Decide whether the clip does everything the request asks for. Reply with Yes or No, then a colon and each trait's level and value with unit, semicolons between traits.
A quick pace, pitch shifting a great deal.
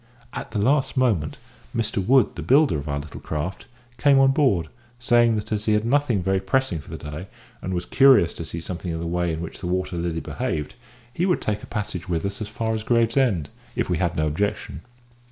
Yes: fast, 225 wpm; wide, 6.1 semitones